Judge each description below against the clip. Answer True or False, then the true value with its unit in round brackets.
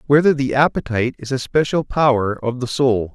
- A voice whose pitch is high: False (130 Hz)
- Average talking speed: True (190 wpm)